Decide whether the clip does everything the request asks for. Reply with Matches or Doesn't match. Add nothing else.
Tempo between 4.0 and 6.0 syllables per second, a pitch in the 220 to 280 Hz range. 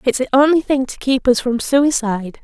Matches